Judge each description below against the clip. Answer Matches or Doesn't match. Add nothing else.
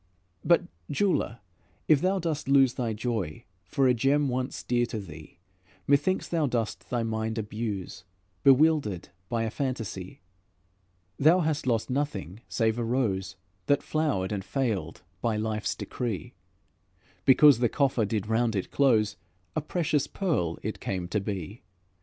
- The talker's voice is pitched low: Matches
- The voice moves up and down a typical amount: Matches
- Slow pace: Doesn't match